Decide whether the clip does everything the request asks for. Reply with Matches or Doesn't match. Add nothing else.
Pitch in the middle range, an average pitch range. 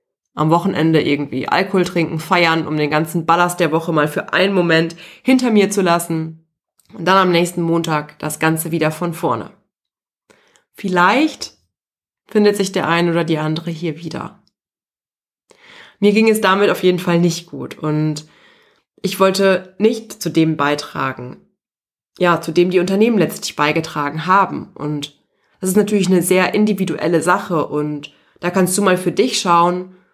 Matches